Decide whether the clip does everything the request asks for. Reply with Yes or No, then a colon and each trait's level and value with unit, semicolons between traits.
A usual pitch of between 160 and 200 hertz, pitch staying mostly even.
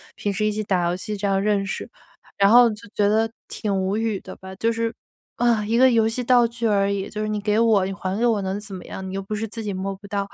No: high, 210 Hz; narrow, 2.3 semitones